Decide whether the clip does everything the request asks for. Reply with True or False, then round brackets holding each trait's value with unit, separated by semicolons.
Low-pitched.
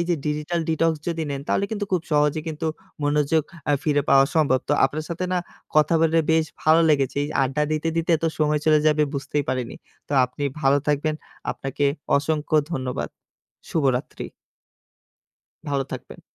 False (150 Hz)